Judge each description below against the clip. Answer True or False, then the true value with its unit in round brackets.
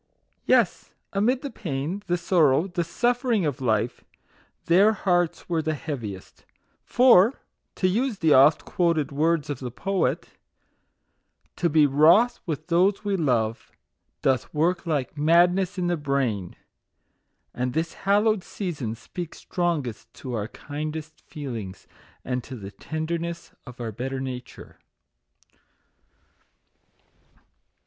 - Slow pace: True (130 wpm)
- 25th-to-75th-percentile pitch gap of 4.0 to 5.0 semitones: False (5.5 semitones)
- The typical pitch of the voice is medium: True (160 Hz)